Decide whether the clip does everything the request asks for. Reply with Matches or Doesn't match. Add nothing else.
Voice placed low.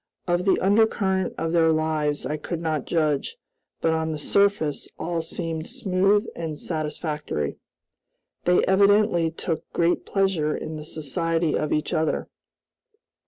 Doesn't match